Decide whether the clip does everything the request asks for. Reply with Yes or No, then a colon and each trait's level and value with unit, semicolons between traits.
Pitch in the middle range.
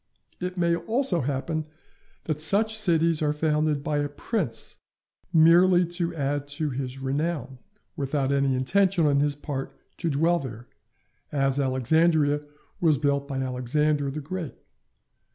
Yes: medium, 150 Hz